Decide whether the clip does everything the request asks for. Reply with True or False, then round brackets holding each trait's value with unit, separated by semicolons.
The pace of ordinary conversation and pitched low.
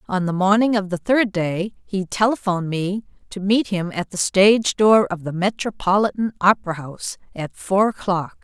False (180 wpm; 195 Hz)